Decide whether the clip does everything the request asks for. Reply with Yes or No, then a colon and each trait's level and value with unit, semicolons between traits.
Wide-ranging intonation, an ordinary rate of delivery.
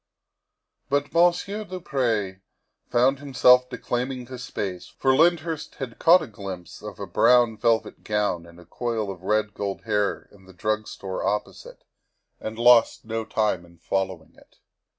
No: average, 4.8 semitones; average, 155 wpm